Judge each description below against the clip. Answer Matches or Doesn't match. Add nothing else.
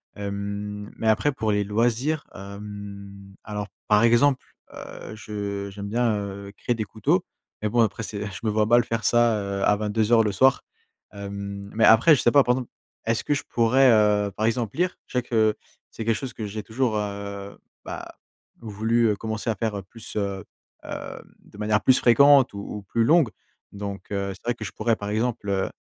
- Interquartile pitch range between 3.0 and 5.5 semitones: Doesn't match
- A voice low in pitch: Matches